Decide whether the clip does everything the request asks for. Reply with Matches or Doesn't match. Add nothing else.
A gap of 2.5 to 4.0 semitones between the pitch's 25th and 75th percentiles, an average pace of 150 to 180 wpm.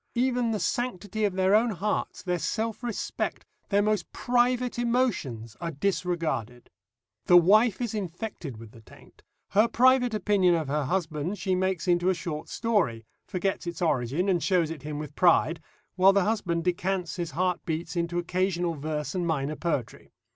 Doesn't match